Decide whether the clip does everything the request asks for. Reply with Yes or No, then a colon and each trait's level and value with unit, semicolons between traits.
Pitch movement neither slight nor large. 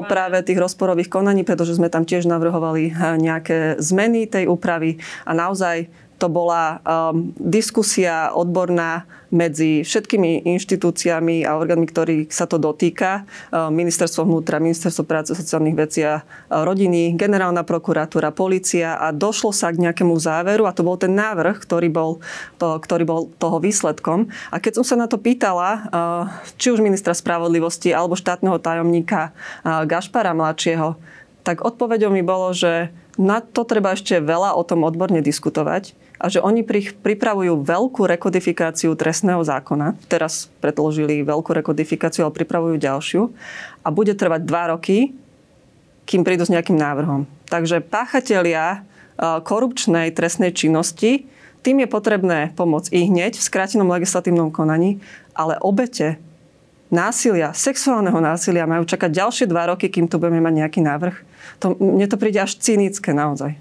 Yes: average, 3.1 semitones